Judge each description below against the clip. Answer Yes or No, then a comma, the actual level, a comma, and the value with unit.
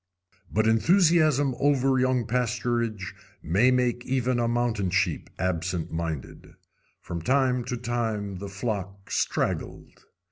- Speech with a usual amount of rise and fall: Yes, average, 4.6 semitones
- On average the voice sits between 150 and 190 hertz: No, low, 120 Hz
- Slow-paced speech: Yes, slow, 115 wpm